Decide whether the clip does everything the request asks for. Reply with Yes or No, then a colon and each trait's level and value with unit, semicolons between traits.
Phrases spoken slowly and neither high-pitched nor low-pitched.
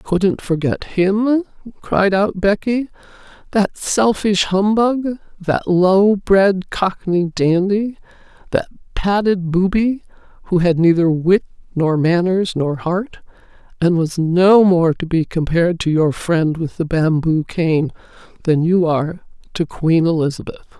Yes: slow, 130 wpm; medium, 180 Hz